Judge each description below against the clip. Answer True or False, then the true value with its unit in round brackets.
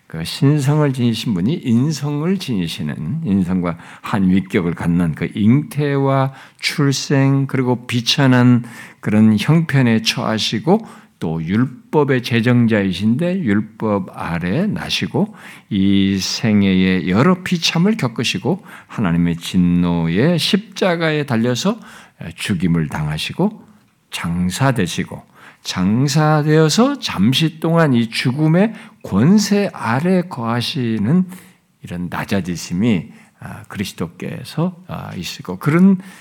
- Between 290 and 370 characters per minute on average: False (235 characters per minute)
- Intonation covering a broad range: True (8.9 semitones)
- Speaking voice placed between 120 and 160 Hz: True (135 Hz)